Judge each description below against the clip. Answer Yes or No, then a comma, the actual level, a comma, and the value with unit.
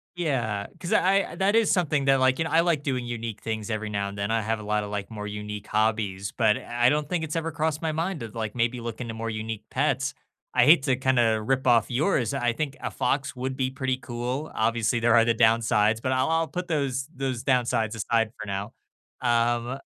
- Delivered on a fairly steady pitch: No, average, 3.9 semitones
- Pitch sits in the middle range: No, low, 120 Hz